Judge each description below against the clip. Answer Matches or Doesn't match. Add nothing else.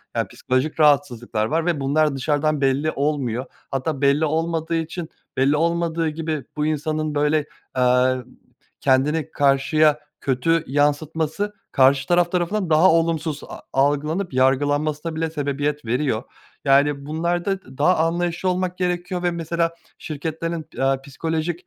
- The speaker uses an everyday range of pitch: Matches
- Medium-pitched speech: Matches